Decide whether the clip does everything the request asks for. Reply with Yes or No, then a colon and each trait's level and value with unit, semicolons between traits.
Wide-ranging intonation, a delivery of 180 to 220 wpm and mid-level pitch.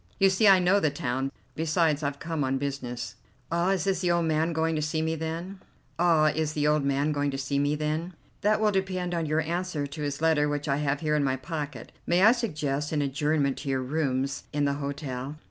No: average, 3.1 semitones; average, 185 wpm; medium, 150 Hz